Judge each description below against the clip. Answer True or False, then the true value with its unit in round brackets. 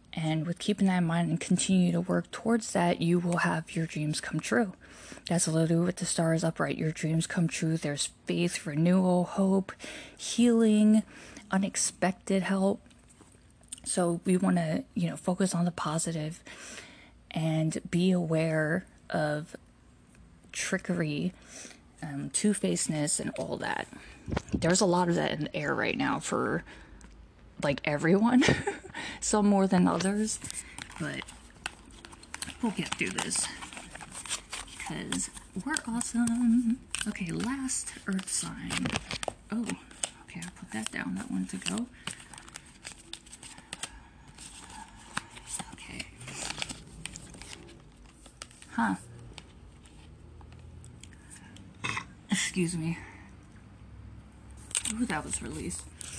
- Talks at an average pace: False (110 wpm)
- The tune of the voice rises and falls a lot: False (4.5 semitones)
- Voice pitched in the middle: True (175 Hz)